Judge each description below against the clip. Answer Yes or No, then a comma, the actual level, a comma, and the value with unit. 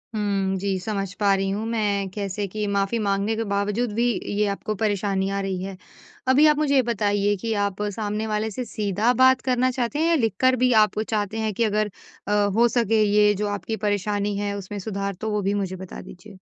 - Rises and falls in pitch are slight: Yes, narrow, 2.0 semitones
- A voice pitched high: Yes, high, 210 Hz